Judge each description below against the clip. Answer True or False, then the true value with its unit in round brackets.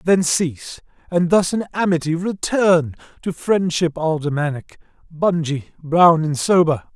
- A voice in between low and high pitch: True (170 Hz)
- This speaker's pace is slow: True (120 wpm)